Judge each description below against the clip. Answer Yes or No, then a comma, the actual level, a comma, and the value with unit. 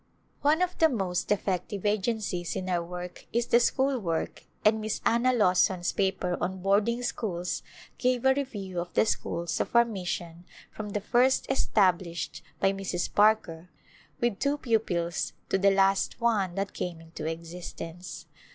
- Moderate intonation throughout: Yes, average, 4.7 semitones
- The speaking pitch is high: Yes, high, 195 Hz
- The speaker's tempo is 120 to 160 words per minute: Yes, average, 155 wpm